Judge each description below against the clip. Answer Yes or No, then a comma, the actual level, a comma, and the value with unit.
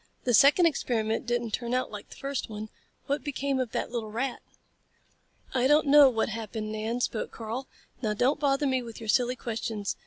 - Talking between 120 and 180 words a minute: No, average, 190 wpm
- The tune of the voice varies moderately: Yes, average, 3.5 semitones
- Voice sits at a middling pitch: No, high, 240 Hz